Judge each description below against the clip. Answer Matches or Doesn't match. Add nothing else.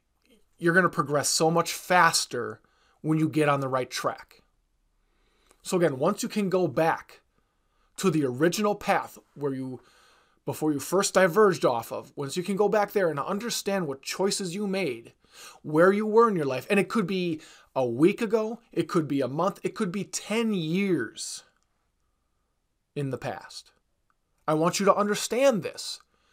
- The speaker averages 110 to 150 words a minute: Doesn't match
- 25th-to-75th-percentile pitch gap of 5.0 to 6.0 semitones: Matches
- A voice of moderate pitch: Matches